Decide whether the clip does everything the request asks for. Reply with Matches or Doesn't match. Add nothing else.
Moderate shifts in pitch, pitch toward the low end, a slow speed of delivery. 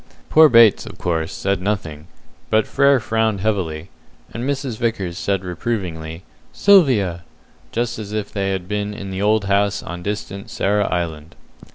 Doesn't match